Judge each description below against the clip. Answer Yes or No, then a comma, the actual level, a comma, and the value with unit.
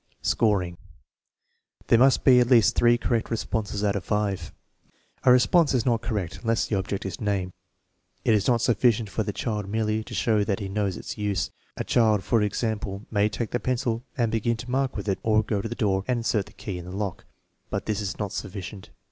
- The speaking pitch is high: No, low, 110 Hz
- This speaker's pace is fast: Yes, fast, 215 wpm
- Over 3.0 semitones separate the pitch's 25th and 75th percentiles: No, average, 2.7 semitones